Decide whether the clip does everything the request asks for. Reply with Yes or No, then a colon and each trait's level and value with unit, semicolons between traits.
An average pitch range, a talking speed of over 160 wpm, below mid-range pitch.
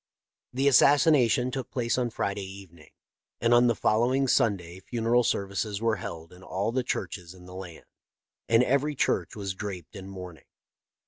Yes: average, 4.6 semitones; average, 170 wpm; low, 105 Hz